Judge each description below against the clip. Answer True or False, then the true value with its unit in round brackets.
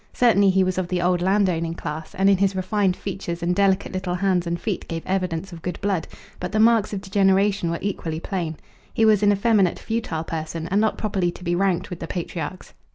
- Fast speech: True (220 wpm)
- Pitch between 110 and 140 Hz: False (185 Hz)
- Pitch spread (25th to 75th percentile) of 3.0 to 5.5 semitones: False (2.6 semitones)